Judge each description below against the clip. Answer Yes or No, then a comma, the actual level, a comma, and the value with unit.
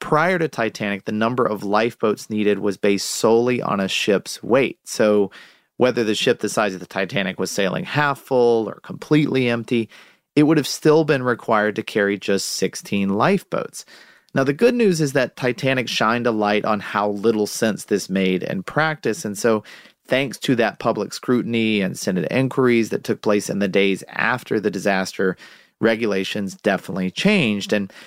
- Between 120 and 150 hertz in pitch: No, low, 110 Hz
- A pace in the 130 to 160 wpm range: No, average, 175 wpm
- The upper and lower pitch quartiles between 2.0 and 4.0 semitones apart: No, average, 4.6 semitones